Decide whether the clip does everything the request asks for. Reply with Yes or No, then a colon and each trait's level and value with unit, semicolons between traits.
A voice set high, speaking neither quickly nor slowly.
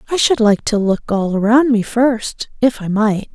No: high, 225 Hz; fast, 215 wpm